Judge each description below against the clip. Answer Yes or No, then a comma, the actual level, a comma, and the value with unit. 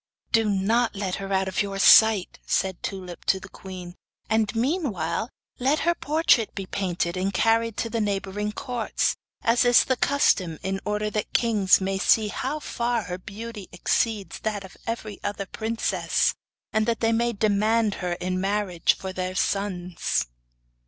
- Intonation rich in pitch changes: No, average, 3.1 semitones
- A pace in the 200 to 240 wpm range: No, average, 165 wpm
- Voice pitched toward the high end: Yes, high, 205 Hz